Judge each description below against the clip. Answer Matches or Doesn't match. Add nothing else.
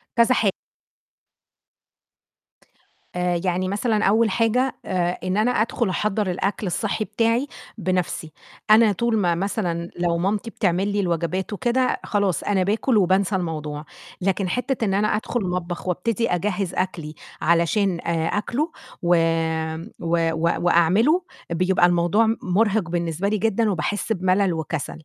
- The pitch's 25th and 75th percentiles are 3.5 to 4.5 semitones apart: Matches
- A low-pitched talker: Doesn't match